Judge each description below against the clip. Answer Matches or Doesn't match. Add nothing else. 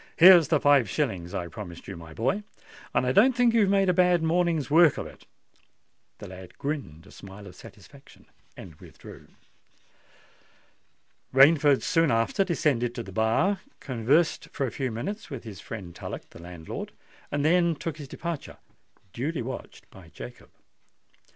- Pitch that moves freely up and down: Matches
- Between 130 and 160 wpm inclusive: Matches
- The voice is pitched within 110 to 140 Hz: Matches